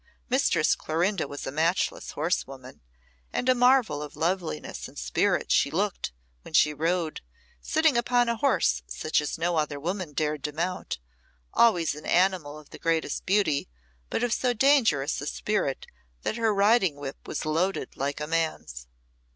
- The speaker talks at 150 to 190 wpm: Yes, average, 160 wpm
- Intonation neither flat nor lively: No, wide, 6.0 semitones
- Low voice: No, medium, 165 Hz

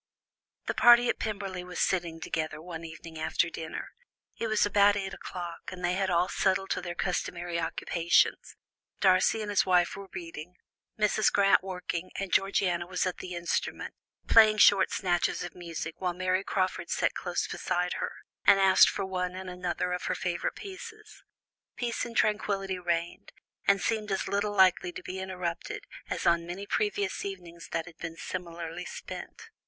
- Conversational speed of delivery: Yes, average, 170 wpm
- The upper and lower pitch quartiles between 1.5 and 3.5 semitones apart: Yes, narrow, 2.5 semitones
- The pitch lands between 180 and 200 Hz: Yes, medium, 185 Hz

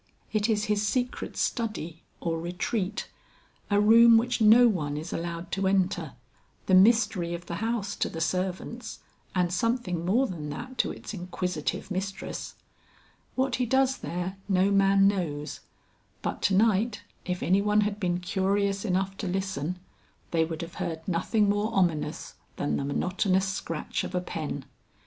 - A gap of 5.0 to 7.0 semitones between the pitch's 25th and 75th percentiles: No, average, 3.4 semitones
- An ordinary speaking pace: Yes, average, 160 wpm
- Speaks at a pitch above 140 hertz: Yes, high, 190 Hz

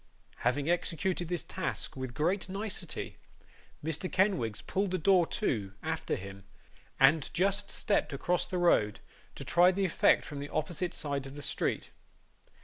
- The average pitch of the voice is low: No, medium, 165 Hz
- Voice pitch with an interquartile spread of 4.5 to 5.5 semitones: Yes, average, 5.2 semitones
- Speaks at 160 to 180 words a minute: No, average, 150 wpm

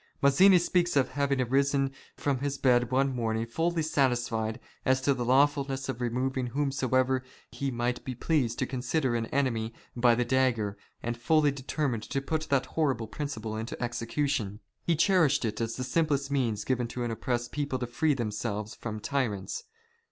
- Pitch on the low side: Yes, low, 130 Hz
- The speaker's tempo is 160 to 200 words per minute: Yes, average, 175 wpm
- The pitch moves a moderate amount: Yes, average, 3.1 semitones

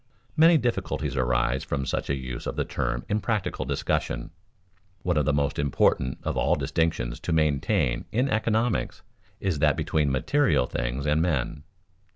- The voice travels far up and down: Yes, wide, 6.9 semitones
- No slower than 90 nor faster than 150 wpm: No, average, 160 wpm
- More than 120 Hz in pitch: No, very low, 75 Hz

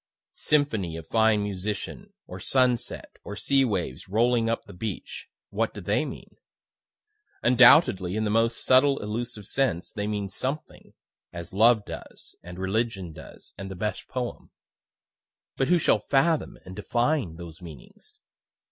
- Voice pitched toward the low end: Yes, low, 110 Hz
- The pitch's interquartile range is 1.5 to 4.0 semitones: No, average, 4.8 semitones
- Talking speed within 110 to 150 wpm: Yes, average, 145 wpm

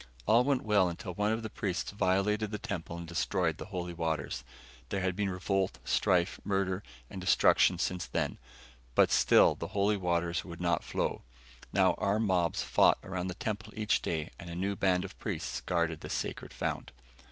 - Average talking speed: Yes, average, 185 wpm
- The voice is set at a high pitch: No, very low, 95 Hz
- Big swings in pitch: No, average, 2.8 semitones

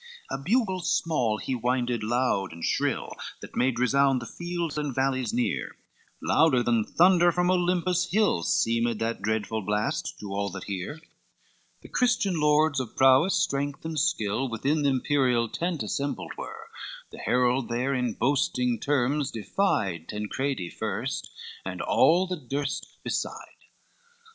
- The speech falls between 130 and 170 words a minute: Yes, average, 145 wpm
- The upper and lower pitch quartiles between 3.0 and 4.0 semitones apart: No, wide, 5.6 semitones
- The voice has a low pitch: Yes, low, 130 Hz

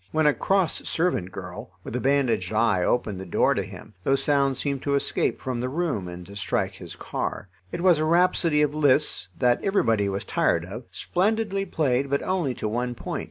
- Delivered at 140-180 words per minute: No, fast, 205 wpm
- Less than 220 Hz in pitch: Yes, low, 135 Hz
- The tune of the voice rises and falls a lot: Yes, wide, 6.6 semitones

